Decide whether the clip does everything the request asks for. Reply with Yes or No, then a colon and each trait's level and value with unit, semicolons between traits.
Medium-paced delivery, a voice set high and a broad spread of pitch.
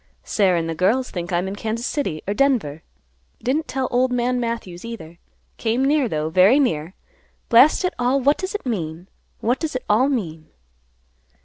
Yes: average, 185 wpm; high, 230 Hz; wide, 6.8 semitones